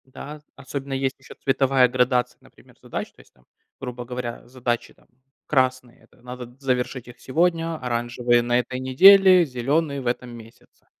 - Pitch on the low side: Yes, low, 130 Hz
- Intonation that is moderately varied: No, narrow, 2.0 semitones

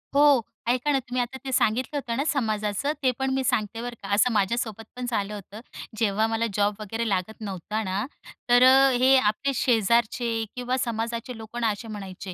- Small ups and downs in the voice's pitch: No, average, 3.2 semitones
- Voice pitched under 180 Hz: No, high, 230 Hz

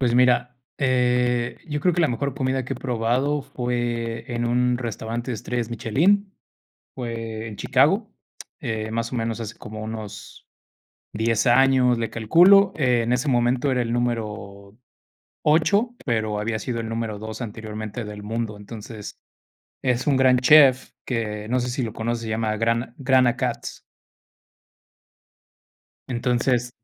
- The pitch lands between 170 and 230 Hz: No, low, 120 Hz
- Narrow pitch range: Yes, narrow, 2.3 semitones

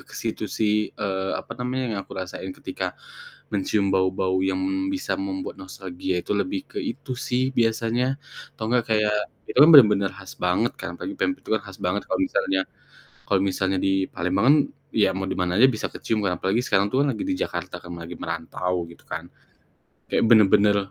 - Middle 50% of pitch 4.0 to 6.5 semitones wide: Yes, average, 4.7 semitones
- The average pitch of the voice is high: No, low, 100 Hz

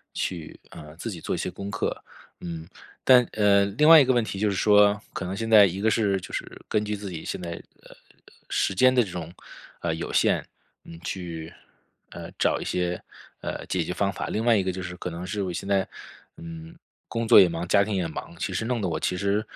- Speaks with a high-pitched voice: No, low, 100 Hz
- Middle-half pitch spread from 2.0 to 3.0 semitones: No, average, 3.6 semitones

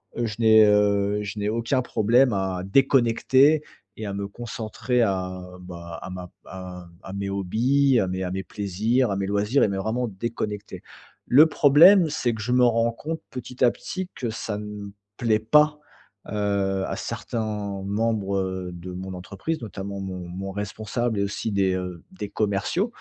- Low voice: Yes, low, 105 Hz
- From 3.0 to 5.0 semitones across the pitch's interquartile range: Yes, average, 3.6 semitones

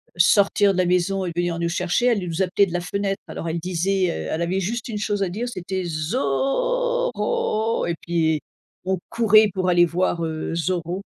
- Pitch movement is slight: No, average, 3.2 semitones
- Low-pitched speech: No, medium, 185 Hz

